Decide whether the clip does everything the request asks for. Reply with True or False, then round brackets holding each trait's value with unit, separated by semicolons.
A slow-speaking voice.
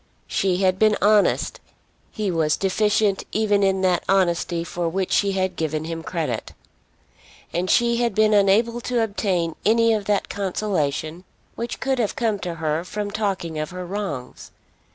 False (160 wpm)